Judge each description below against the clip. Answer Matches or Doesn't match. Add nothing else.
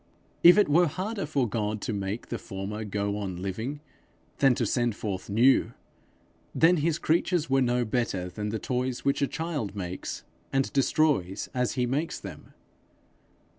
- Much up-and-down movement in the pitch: Matches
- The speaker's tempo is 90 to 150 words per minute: Doesn't match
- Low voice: Matches